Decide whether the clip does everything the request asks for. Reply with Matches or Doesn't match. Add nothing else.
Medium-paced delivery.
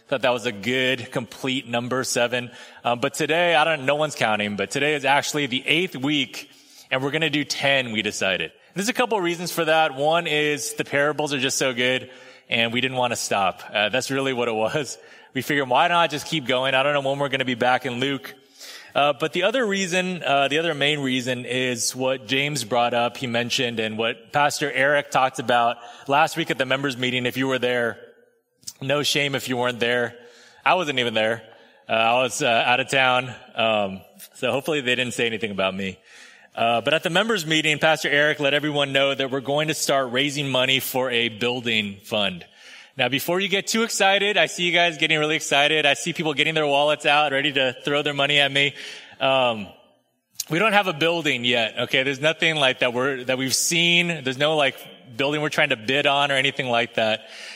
Doesn't match